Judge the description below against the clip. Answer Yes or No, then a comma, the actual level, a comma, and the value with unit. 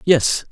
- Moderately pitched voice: Yes, medium, 145 Hz